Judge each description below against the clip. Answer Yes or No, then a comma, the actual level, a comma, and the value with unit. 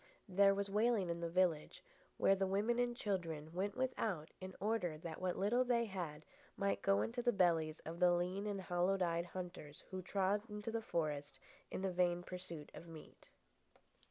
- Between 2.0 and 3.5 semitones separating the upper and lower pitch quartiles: Yes, average, 3.1 semitones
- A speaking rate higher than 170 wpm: Yes, average, 180 wpm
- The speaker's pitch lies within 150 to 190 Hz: Yes, medium, 185 Hz